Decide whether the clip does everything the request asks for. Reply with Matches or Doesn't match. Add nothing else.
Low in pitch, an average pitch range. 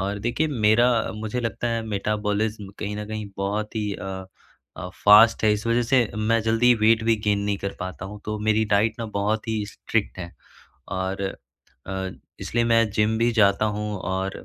Doesn't match